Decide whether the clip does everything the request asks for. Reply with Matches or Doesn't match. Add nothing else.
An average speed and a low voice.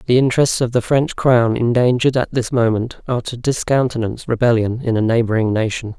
Matches